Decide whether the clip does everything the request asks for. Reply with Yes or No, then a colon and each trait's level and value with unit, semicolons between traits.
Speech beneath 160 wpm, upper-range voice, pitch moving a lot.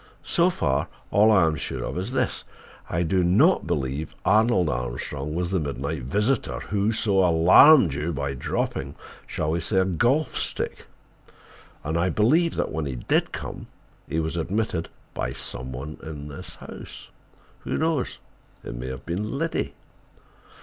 No: average, 150 wpm; very low, 85 Hz; wide, 6.8 semitones